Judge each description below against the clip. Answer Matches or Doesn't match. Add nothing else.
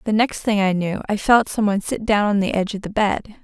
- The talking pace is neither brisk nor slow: Doesn't match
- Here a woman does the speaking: Matches